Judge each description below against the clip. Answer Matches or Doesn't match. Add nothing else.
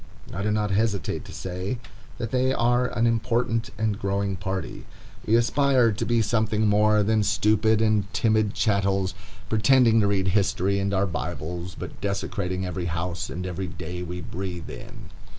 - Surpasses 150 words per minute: Matches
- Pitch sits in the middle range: Doesn't match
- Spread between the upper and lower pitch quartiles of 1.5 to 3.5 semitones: Matches